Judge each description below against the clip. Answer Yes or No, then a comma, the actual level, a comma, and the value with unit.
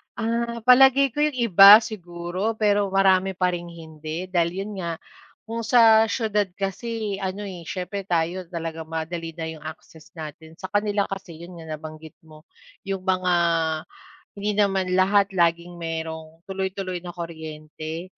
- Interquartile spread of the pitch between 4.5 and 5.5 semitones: No, average, 3.6 semitones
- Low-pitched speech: No, medium, 185 Hz